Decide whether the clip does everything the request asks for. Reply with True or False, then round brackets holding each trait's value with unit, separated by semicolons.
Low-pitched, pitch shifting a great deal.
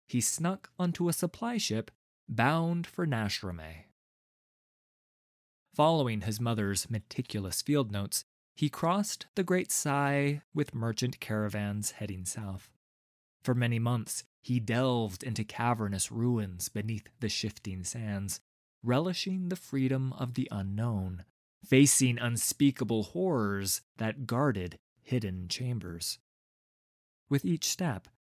True (120 Hz; 5.7 semitones)